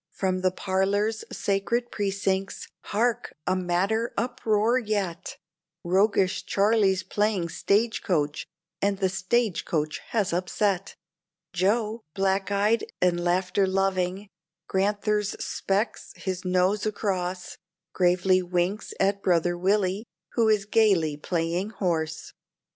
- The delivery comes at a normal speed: No, slow, 115 wpm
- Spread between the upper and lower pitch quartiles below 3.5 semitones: Yes, narrow, 2.5 semitones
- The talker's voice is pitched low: No, high, 195 Hz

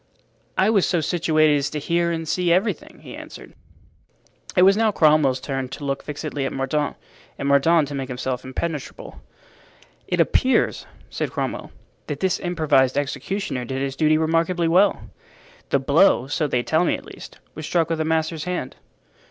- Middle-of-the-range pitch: Yes, medium, 155 Hz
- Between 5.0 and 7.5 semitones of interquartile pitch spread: No, average, 3.8 semitones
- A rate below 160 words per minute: No, average, 170 wpm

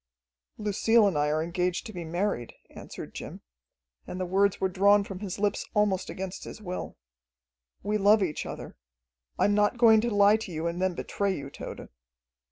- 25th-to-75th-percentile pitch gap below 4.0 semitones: Yes, average, 2.7 semitones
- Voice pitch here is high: Yes, high, 195 Hz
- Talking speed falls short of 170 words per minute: No, average, 185 wpm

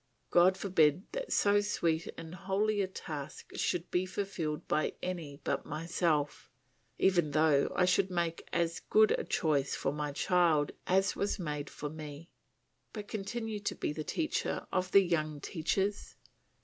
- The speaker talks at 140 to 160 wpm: Yes, average, 155 wpm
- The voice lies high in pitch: No, medium, 175 Hz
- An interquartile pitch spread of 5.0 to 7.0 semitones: No, average, 4.1 semitones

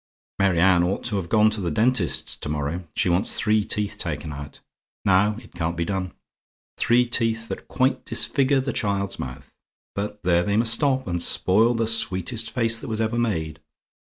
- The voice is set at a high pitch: No, low, 105 Hz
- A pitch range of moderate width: Yes, average, 4.6 semitones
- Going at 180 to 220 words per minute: Yes, average, 185 wpm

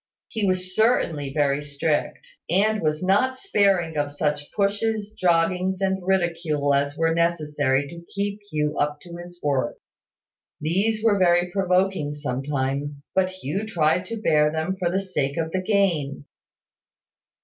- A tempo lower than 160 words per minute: Yes, average, 145 wpm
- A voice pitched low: No, medium, 170 Hz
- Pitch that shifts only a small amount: No, average, 4.5 semitones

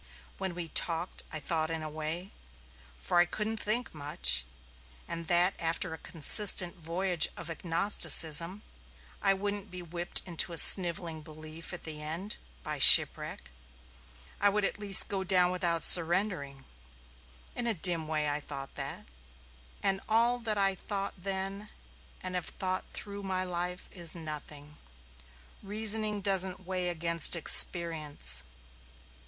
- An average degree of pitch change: Yes, average, 3.3 semitones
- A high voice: No, medium, 175 Hz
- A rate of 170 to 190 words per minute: No, slow, 135 wpm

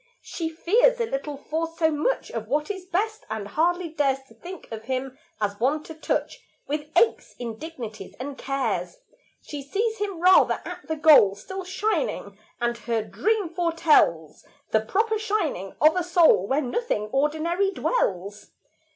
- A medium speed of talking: Yes, average, 160 wpm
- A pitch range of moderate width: No, wide, 7.2 semitones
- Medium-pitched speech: No, very high, 310 Hz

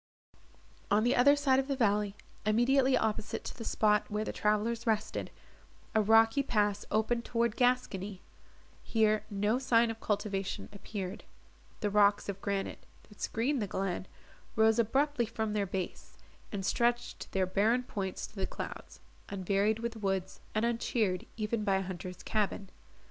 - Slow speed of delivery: No, average, 155 wpm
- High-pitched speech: Yes, high, 215 Hz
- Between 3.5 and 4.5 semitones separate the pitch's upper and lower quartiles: No, average, 2.7 semitones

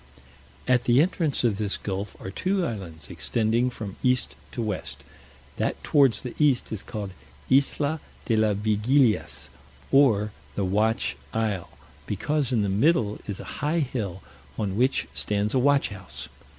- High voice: No, low, 110 Hz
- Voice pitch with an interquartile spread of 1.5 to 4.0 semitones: No, average, 4.6 semitones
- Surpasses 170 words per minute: No, average, 150 wpm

